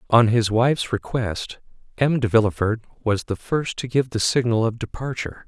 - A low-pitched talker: Yes, low, 115 Hz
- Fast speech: No, average, 175 wpm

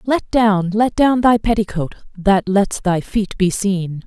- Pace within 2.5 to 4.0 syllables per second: Yes, 3.7 syllables/s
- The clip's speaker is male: No, female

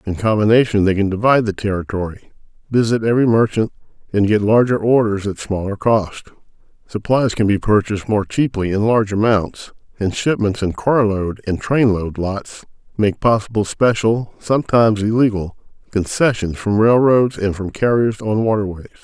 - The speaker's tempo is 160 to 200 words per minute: No, average, 150 wpm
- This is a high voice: No, low, 105 Hz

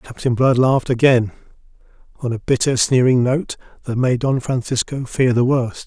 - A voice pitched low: Yes, low, 125 Hz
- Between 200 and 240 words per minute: No, average, 165 wpm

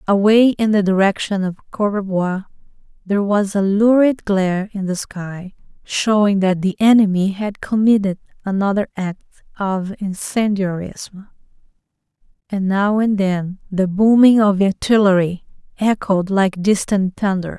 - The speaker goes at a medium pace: No, slow, 125 wpm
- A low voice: No, high, 200 Hz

